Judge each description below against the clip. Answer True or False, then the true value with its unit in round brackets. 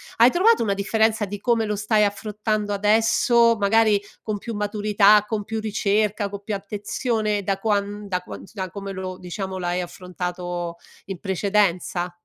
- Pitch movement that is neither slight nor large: False (2.0 semitones)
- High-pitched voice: True (205 Hz)